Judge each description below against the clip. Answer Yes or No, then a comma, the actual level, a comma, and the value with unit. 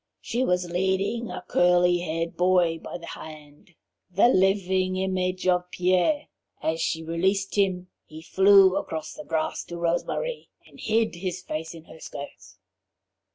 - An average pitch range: No, narrow, 2.3 semitones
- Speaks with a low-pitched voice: No, medium, 180 Hz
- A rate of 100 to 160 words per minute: Yes, average, 155 wpm